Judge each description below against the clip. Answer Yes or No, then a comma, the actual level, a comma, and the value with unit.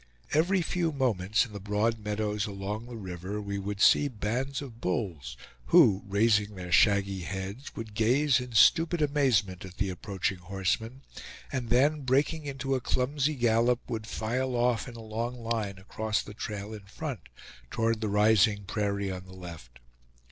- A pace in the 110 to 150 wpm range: No, average, 165 wpm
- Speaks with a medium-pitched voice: No, low, 110 Hz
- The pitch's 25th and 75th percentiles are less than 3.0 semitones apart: No, average, 4.0 semitones